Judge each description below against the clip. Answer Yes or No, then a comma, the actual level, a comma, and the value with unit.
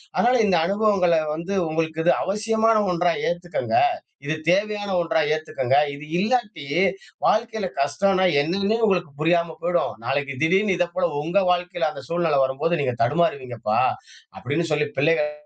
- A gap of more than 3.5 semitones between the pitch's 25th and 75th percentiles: Yes, average, 4.6 semitones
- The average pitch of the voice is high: No, medium, 170 Hz